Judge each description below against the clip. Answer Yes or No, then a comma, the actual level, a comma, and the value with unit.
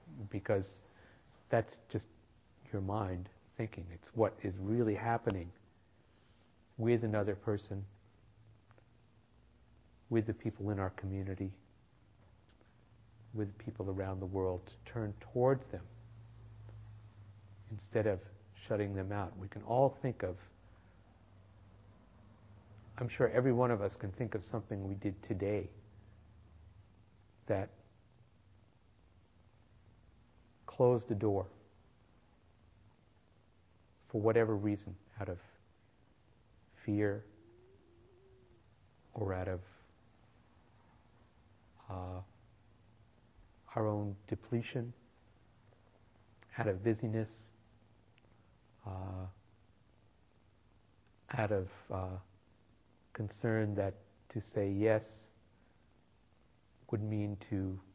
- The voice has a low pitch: Yes, low, 105 Hz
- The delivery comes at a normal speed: No, slow, 85 wpm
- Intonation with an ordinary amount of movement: No, narrow, 2.2 semitones